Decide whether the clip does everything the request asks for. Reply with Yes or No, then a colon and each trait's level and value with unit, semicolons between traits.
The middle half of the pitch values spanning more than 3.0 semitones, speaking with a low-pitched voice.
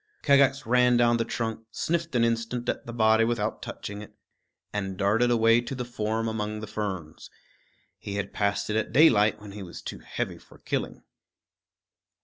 No: narrow, 2.5 semitones; low, 110 Hz